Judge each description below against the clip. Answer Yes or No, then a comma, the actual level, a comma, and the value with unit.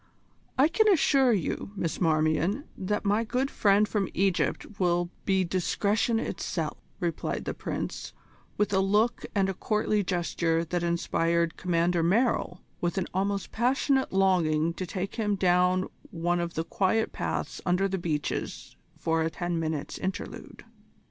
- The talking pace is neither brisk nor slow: Yes, average, 150 wpm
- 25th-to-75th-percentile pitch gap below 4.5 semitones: Yes, average, 3.5 semitones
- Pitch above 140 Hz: Yes, medium, 185 Hz